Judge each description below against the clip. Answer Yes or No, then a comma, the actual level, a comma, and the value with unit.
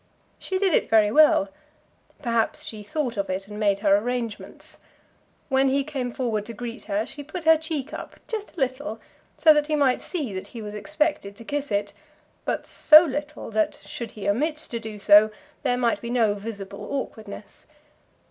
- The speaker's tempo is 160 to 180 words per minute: No, average, 190 wpm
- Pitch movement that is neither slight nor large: No, wide, 5.9 semitones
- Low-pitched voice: No, high, 235 Hz